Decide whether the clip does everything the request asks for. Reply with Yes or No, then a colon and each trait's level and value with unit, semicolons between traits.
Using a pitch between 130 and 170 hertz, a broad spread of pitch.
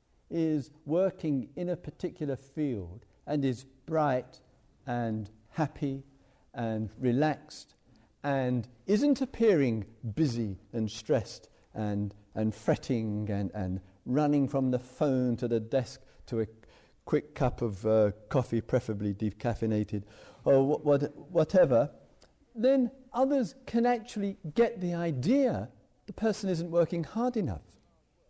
Yes: low, 135 Hz; wide, 6.8 semitones